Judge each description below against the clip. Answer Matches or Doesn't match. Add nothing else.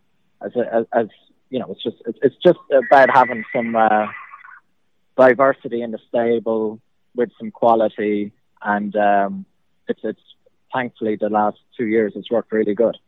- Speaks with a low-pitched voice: Matches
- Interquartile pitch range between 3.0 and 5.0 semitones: Doesn't match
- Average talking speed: Matches